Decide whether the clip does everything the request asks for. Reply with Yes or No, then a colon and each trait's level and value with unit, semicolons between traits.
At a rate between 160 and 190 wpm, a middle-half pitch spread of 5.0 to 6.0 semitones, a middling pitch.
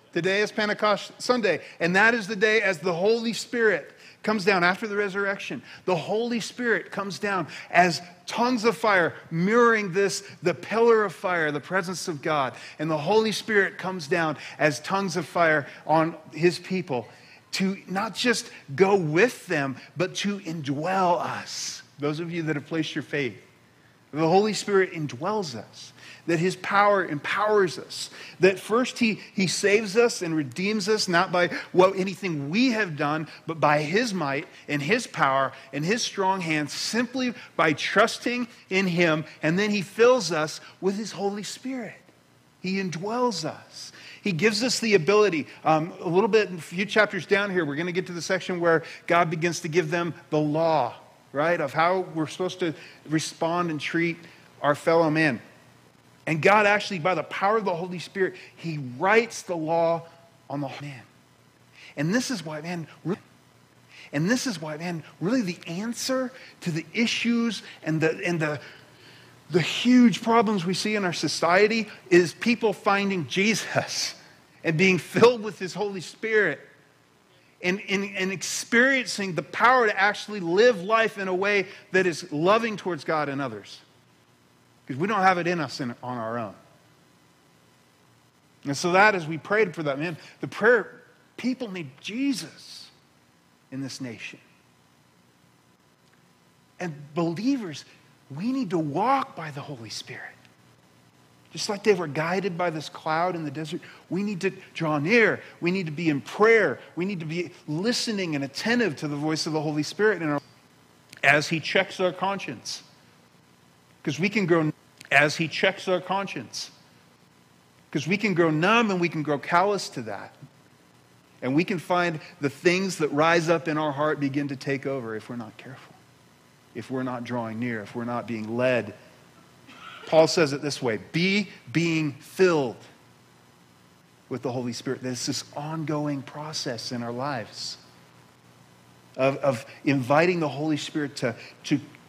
Yes: average, 170 wpm; wide, 5.4 semitones; medium, 175 Hz